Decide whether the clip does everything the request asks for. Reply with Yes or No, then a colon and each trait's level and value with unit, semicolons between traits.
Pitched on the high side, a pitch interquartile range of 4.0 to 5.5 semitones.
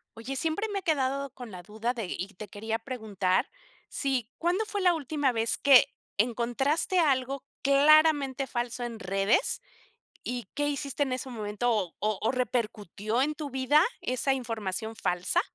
Yes: very high, 250 Hz; average, 4.4 semitones